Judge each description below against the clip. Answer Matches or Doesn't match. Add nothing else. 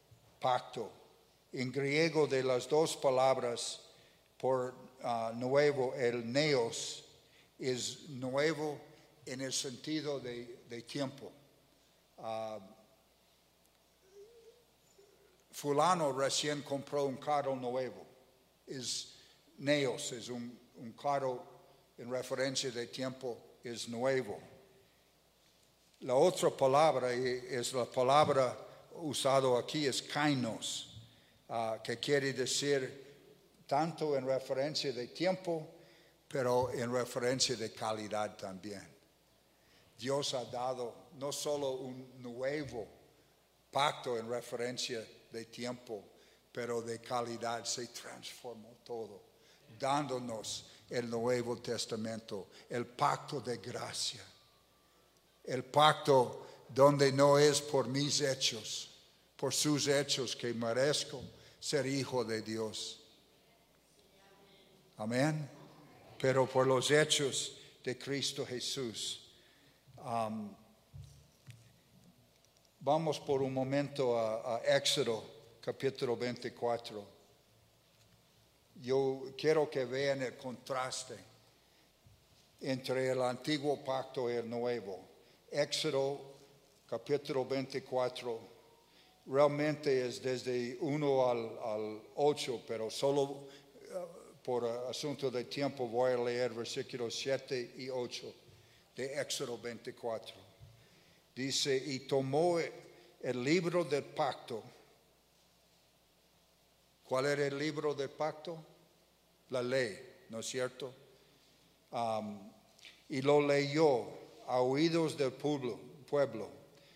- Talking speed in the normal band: Doesn't match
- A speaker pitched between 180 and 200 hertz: Doesn't match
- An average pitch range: Matches